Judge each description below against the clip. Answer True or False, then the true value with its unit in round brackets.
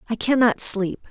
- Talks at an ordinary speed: False (215 wpm)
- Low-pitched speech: False (225 Hz)